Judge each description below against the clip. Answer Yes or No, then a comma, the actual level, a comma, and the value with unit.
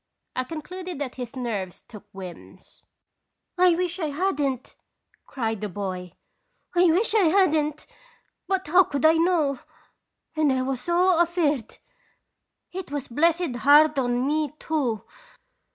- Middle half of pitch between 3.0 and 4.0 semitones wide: No, wide, 5.6 semitones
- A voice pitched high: Yes, very high, 295 Hz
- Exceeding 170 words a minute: No, slow, 135 wpm